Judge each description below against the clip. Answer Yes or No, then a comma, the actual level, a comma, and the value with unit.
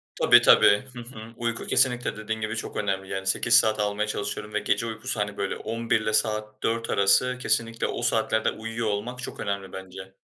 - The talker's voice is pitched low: Yes, low, 110 Hz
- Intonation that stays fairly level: Yes, narrow, 2.1 semitones